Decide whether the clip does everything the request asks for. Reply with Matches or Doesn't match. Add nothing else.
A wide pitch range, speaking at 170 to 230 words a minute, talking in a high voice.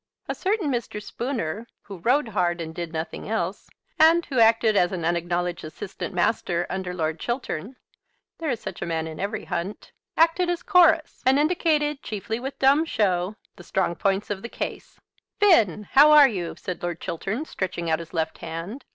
Matches